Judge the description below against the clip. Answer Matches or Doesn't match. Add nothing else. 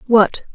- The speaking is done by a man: Doesn't match